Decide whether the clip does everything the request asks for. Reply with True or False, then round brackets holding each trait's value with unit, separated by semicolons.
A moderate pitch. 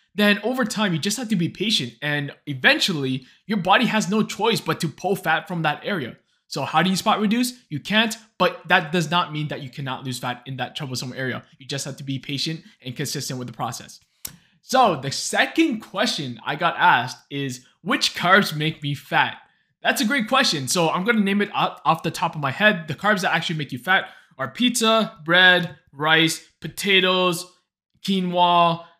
True (170 Hz)